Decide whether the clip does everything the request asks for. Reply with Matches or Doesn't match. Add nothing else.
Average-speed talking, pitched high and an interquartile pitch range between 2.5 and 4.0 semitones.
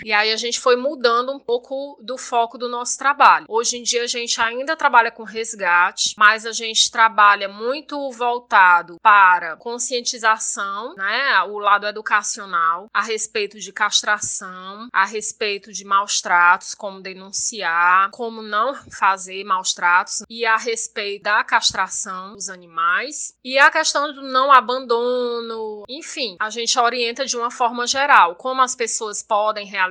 Matches